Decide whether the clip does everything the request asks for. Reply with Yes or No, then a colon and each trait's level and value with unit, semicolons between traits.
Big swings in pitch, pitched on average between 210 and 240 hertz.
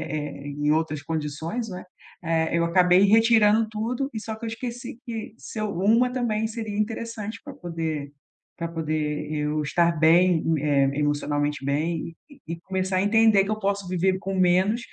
No: wide, 5.8 semitones; medium, 185 Hz